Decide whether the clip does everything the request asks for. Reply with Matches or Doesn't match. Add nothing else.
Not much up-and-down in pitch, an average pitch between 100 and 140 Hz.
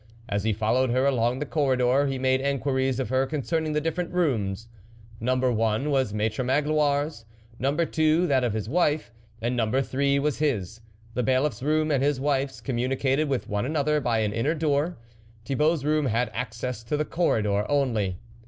Doesn't match